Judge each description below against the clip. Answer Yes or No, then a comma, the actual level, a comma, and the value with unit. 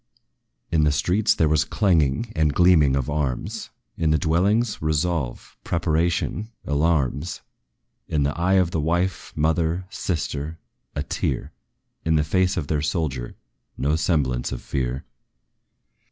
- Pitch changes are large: No, average, 3.2 semitones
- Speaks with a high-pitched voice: No, very low, 80 Hz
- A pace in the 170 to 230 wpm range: No, slow, 135 wpm